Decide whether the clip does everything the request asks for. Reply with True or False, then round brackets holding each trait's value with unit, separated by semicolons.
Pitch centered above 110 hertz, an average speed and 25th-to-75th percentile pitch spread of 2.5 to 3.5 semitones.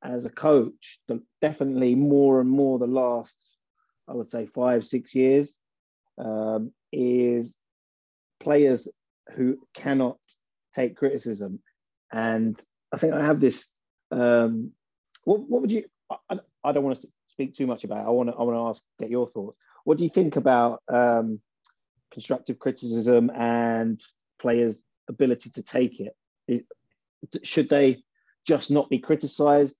True (125 Hz; 150 wpm; 3.2 semitones)